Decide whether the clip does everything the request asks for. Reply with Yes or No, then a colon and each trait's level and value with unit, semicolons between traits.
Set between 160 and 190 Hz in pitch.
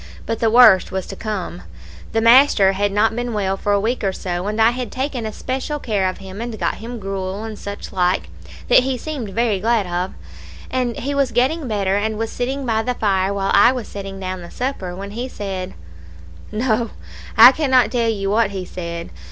No: high, 215 Hz